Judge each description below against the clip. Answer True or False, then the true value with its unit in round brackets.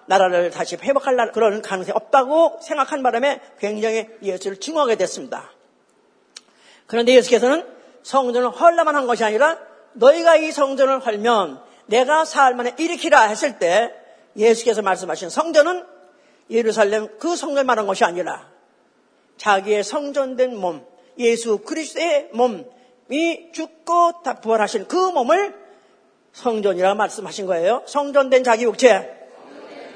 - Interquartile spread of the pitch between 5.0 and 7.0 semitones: True (5.3 semitones)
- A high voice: True (250 Hz)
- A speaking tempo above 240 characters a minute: True (300 characters per minute)